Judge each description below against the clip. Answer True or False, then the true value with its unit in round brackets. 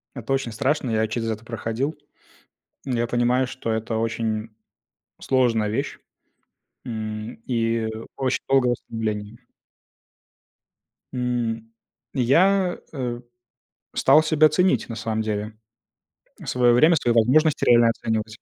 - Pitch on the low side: True (120 Hz)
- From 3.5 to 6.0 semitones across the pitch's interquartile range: False (2.8 semitones)